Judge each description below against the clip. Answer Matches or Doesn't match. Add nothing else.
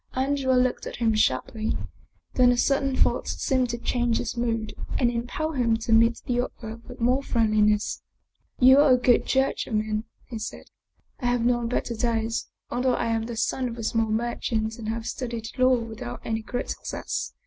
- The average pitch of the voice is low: Doesn't match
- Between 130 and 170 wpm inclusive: Doesn't match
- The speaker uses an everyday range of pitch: Doesn't match